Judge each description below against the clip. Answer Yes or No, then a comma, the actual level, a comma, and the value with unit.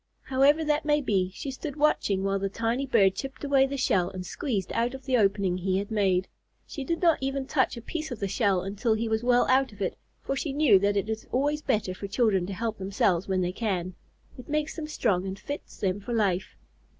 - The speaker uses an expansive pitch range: Yes, wide, 5.8 semitones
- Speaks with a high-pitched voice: Yes, high, 220 Hz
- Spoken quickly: Yes, fast, 235 wpm